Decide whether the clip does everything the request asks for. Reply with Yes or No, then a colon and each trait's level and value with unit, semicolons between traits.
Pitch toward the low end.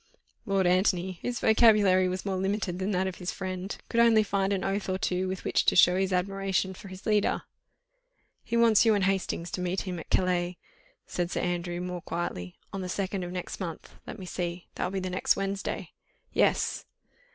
No: medium, 185 Hz